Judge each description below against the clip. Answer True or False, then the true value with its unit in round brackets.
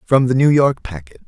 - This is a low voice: True (125 Hz)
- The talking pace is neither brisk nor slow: False (235 wpm)